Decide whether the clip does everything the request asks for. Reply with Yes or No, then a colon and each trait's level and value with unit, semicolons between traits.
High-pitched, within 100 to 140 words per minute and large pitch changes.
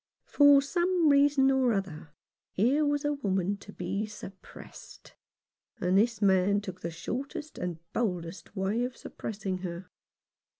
Yes: high, 205 Hz; slow, 135 wpm; wide, 6.8 semitones